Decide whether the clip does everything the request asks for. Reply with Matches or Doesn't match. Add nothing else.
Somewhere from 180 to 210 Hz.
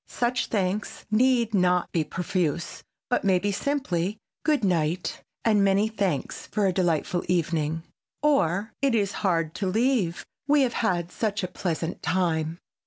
Matches